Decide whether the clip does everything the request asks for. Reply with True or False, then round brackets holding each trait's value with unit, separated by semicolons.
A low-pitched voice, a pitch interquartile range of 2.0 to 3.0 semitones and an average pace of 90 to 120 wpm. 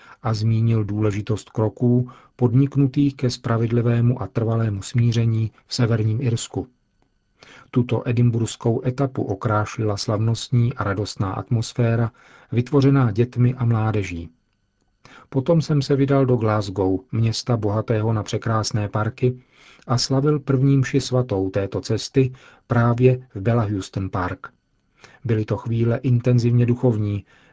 True (115 Hz; 2.7 semitones; 115 wpm)